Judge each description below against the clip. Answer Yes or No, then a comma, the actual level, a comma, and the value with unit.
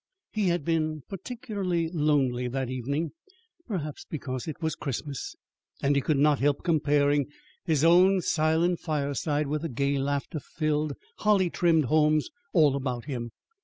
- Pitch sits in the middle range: Yes, medium, 150 Hz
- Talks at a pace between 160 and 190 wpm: No, average, 145 wpm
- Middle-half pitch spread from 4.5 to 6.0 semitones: No, average, 3.0 semitones